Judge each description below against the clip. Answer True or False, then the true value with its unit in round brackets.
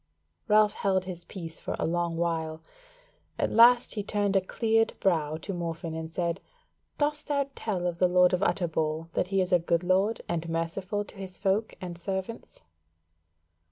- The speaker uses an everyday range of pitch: True (3.3 semitones)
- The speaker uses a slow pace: False (175 wpm)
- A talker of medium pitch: True (180 Hz)